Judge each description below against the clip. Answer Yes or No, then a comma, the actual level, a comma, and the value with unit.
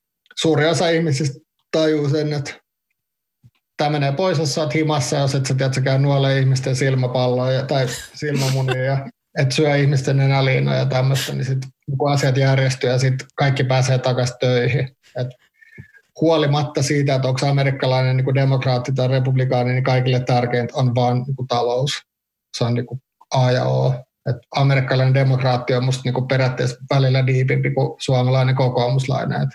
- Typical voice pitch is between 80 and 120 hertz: No, low, 135 Hz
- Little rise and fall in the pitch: Yes, narrow, 1.8 semitones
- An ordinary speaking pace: No, fast, 160 wpm